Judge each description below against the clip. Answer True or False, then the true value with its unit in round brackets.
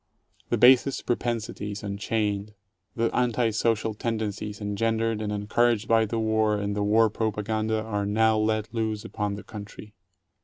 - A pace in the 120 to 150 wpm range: True (145 wpm)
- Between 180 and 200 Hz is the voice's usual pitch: False (110 Hz)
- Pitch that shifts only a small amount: True (1.5 semitones)